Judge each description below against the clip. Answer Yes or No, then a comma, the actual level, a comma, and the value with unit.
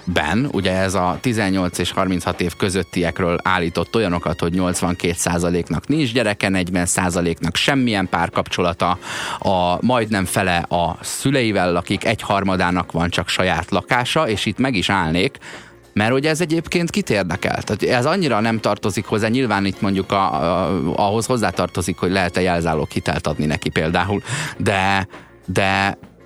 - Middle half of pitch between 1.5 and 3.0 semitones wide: No, average, 3.8 semitones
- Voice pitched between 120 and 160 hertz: No, very low, 95 Hz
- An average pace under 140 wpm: No, average, 145 wpm